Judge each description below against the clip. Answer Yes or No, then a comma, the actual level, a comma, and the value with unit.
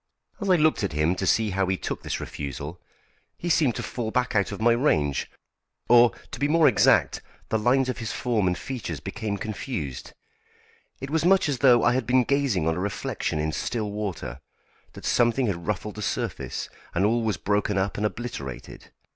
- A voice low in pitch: Yes, low, 110 Hz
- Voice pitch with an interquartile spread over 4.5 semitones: Yes, average, 5.1 semitones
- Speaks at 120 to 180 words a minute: No, average, 195 wpm